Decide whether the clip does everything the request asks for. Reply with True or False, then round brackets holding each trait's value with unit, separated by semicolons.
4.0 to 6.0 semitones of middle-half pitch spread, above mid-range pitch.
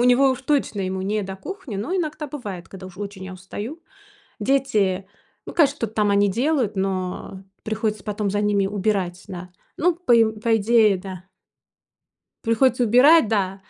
True (4.5 semitones; 210 Hz)